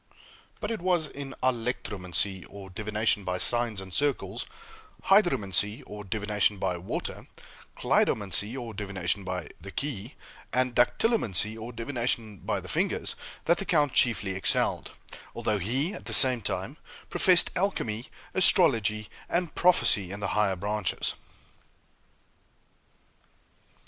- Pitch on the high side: No, low, 110 Hz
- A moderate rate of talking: No, slow, 125 wpm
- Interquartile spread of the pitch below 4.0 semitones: No, wide, 5.4 semitones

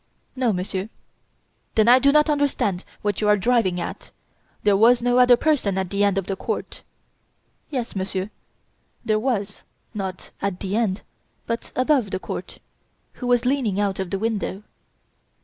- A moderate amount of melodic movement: Yes, average, 4.1 semitones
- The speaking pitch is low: No, high, 210 Hz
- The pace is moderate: Yes, average, 165 wpm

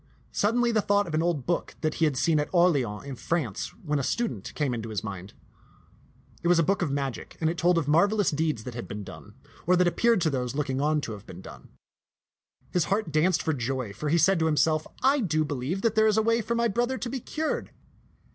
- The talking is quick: Yes, fast, 240 wpm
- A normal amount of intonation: No, wide, 6.5 semitones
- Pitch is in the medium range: Yes, medium, 160 Hz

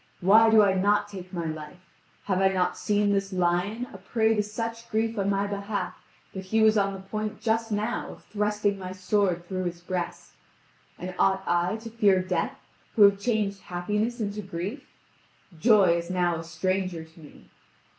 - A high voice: Yes, high, 195 Hz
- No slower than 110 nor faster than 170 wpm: No, average, 185 wpm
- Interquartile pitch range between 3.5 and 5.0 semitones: No, average, 2.7 semitones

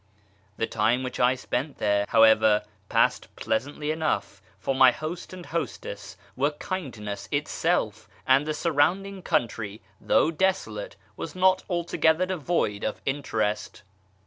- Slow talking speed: Yes, slow, 130 wpm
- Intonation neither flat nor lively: No, wide, 7.4 semitones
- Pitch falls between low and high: Yes, medium, 145 Hz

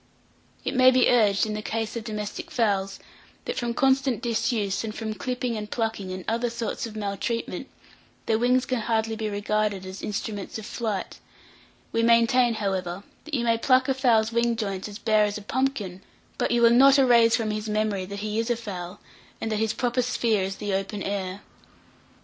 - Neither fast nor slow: Yes, average, 195 wpm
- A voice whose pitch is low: No, high, 220 Hz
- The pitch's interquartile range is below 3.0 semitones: Yes, narrow, 2.6 semitones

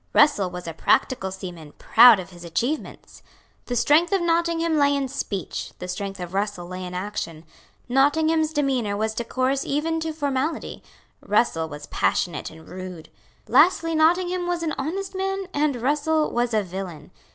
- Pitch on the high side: Yes, very high, 255 Hz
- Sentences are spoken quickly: No, average, 160 wpm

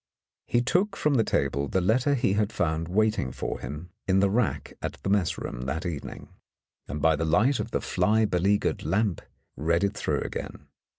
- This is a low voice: Yes, very low, 95 Hz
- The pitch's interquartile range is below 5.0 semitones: No, wide, 5.5 semitones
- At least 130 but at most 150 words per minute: No, average, 190 wpm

